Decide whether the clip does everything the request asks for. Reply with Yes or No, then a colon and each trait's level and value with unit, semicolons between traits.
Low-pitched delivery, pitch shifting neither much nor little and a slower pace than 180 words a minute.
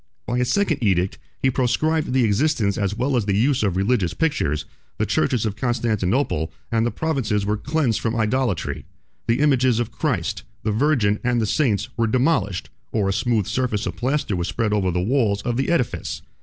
No: low, 115 Hz; average, 4.2 semitones; average, 190 wpm